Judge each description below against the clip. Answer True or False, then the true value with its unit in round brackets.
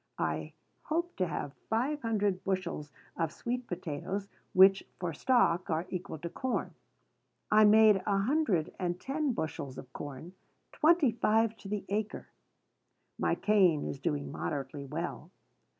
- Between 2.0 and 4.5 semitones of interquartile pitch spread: False (5.5 semitones)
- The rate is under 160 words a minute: True (140 wpm)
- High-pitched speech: True (195 Hz)